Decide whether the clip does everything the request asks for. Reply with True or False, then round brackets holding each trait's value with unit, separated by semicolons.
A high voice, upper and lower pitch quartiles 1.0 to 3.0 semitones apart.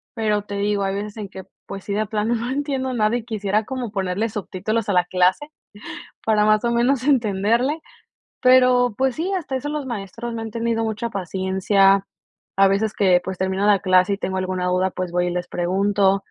False (210 Hz; 3.7 semitones)